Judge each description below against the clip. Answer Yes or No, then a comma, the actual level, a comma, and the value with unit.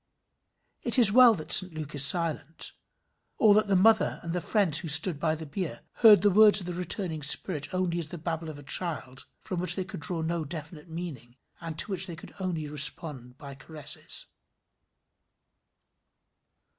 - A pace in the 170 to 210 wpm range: Yes, average, 180 wpm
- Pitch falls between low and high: Yes, medium, 165 Hz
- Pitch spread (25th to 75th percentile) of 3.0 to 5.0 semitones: Yes, average, 3.5 semitones